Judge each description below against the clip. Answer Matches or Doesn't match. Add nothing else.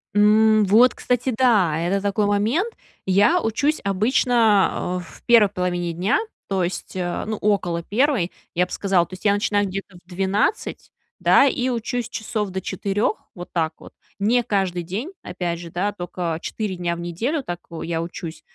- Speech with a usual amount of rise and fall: Matches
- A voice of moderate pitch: Doesn't match